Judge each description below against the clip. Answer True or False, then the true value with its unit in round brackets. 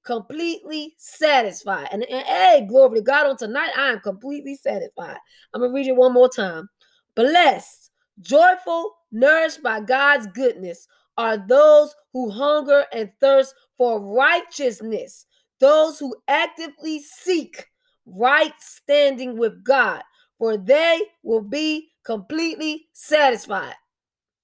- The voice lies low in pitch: False (280 Hz)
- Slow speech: True (125 wpm)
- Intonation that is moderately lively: True (4.5 semitones)